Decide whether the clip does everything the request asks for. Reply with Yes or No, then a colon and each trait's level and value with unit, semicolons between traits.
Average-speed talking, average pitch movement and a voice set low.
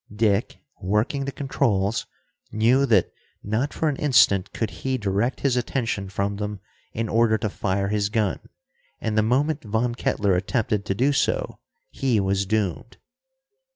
Yes: average, 155 wpm; average, 4.0 semitones; low, 110 Hz